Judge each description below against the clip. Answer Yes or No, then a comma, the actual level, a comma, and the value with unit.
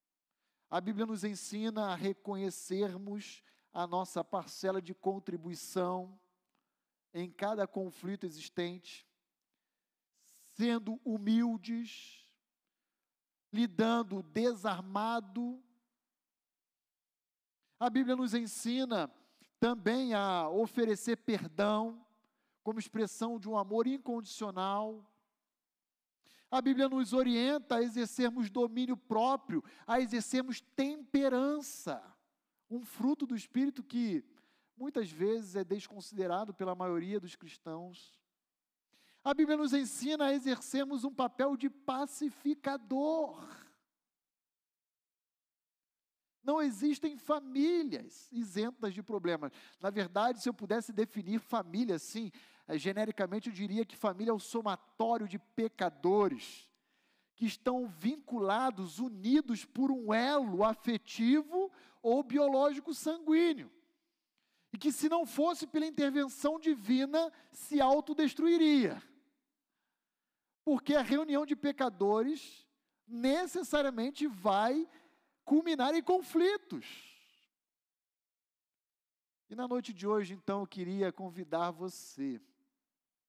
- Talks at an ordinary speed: No, slow, 95 wpm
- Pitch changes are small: No, average, 5.1 semitones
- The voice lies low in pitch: No, high, 240 Hz